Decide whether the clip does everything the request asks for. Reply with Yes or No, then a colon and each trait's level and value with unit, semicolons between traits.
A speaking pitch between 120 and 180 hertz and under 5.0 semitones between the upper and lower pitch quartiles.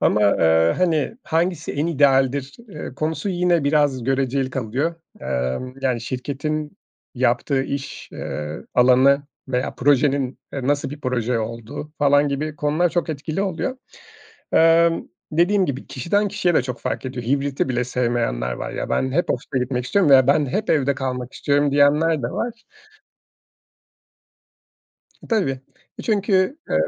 Yes: medium, 140 Hz; average, 4.1 semitones